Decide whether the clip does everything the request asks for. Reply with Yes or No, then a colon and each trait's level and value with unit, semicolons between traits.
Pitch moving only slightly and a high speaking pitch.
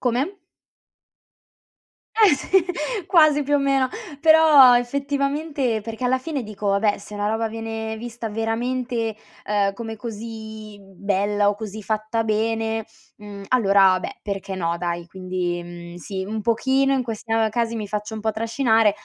No: average, 3.4 semitones; high, 225 Hz